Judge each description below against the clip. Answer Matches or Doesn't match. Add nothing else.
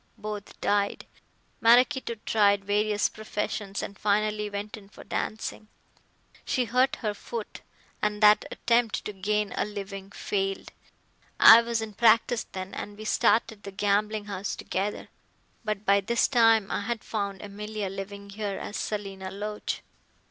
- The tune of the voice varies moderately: Doesn't match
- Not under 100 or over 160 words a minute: Matches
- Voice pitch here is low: Doesn't match